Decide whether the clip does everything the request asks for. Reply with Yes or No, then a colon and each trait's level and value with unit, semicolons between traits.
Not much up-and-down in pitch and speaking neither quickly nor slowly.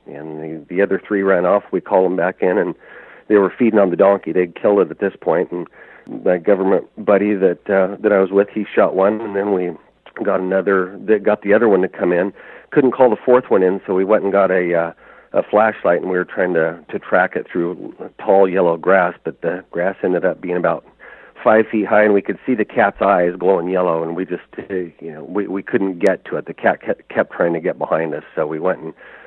No: narrow, 2.0 semitones; fast, 250 wpm